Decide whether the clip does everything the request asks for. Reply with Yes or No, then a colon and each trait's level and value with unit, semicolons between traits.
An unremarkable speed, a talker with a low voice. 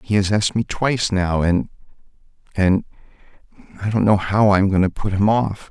Yes: average, 180 wpm; low, 100 Hz